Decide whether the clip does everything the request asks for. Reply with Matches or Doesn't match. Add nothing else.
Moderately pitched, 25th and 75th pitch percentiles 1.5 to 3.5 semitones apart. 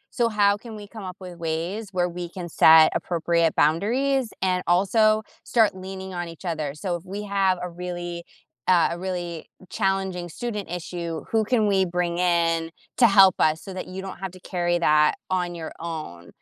Matches